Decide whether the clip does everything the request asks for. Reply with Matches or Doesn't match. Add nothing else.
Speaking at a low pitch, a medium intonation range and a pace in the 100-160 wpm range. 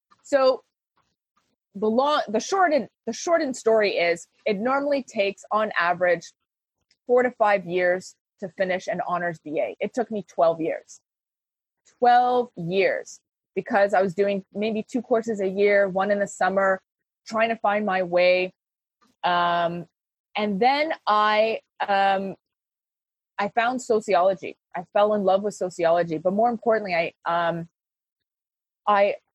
Doesn't match